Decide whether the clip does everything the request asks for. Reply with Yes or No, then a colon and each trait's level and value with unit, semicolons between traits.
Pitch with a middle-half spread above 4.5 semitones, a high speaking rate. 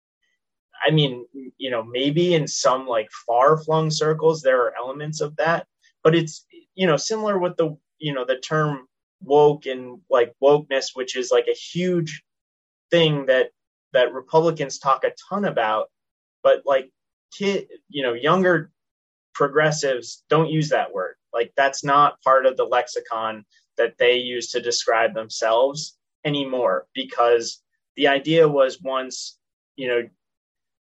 No: average, 5.1 semitones; average, 145 wpm